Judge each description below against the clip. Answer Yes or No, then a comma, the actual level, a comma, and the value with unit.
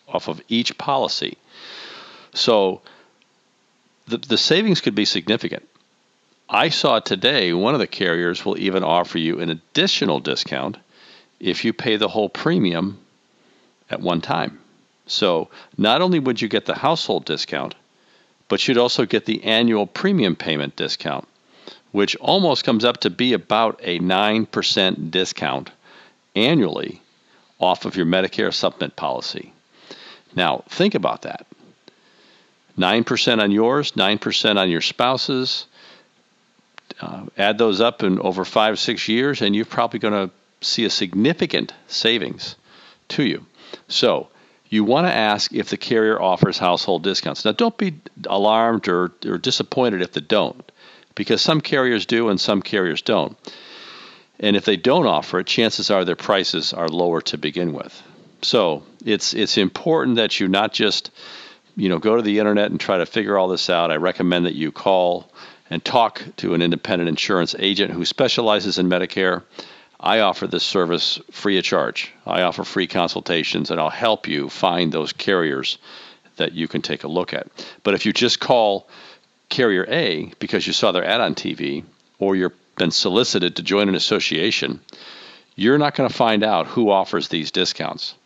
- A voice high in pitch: No, low, 100 Hz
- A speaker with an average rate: Yes, average, 160 wpm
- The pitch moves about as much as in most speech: Yes, average, 4.1 semitones